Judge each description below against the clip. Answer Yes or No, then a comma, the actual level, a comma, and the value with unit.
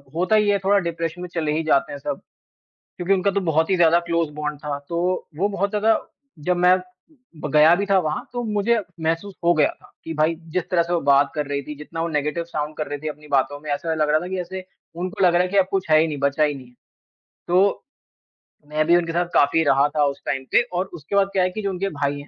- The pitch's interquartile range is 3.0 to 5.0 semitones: Yes, average, 3.6 semitones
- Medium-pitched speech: Yes, medium, 165 Hz